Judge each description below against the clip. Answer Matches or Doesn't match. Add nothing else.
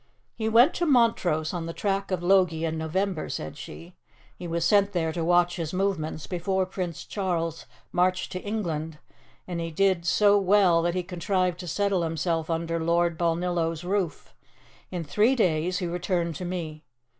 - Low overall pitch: Doesn't match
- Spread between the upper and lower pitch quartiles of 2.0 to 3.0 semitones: Matches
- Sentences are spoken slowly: Doesn't match